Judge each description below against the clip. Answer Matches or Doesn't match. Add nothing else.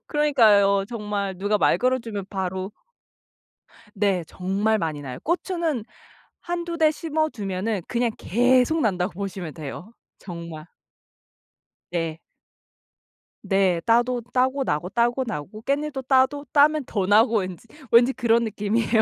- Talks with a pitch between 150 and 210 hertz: Doesn't match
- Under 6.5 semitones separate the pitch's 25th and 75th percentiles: Matches